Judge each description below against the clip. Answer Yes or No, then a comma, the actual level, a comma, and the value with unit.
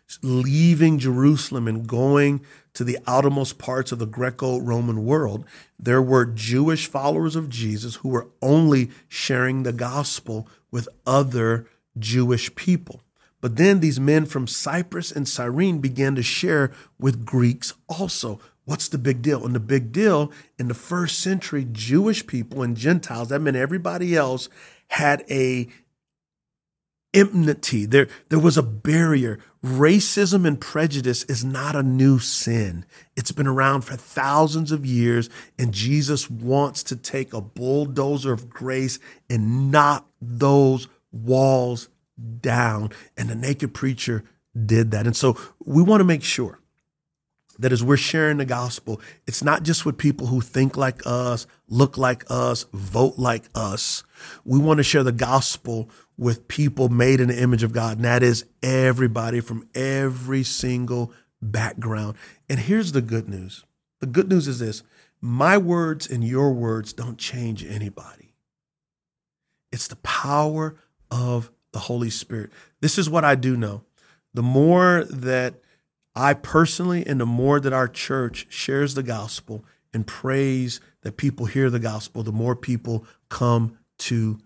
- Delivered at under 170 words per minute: Yes, average, 150 wpm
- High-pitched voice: No, low, 130 Hz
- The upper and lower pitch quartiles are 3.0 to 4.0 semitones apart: Yes, average, 3.5 semitones